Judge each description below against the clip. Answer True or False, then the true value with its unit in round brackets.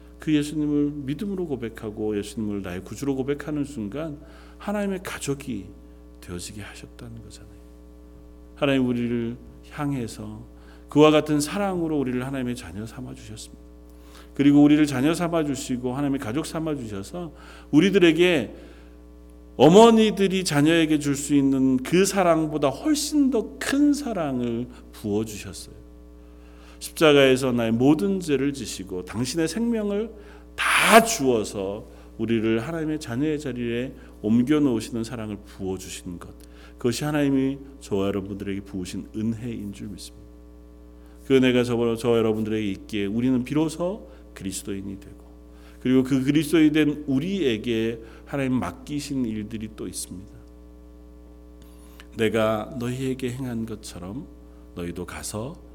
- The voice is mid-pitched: False (115 Hz)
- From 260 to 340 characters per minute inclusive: True (310 characters per minute)